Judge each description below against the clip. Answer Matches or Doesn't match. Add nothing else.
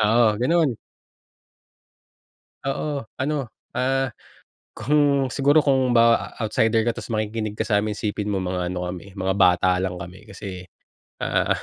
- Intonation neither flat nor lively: Doesn't match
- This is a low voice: Matches